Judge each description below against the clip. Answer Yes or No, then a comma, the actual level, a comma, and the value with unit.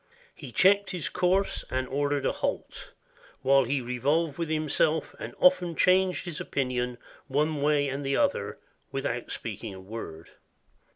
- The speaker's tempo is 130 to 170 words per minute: Yes, average, 155 wpm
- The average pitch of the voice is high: No, medium, 145 Hz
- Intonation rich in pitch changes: No, average, 4.5 semitones